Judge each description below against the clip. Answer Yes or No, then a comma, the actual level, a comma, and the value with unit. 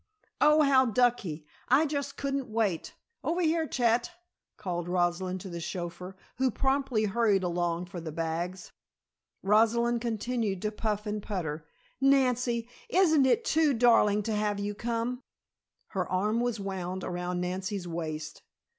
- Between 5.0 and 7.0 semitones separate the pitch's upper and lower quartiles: Yes, wide, 5.5 semitones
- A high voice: Yes, high, 210 Hz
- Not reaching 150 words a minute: Yes, average, 140 wpm